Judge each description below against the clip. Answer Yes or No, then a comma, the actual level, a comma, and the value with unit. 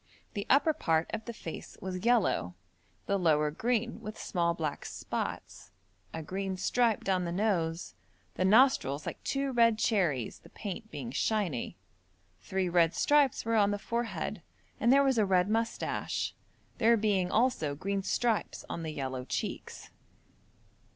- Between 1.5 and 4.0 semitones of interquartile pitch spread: No, wide, 5.4 semitones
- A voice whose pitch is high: Yes, high, 200 Hz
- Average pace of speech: Yes, average, 150 wpm